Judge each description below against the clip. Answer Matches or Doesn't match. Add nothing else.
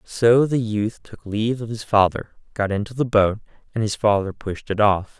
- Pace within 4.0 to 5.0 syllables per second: Matches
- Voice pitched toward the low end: Matches